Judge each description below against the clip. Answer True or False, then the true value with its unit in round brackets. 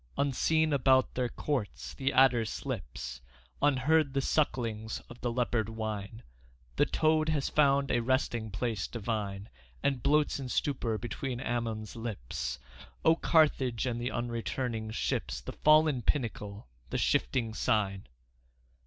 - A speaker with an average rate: False (130 wpm)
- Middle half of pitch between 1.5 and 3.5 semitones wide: False (3.9 semitones)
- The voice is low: True (120 Hz)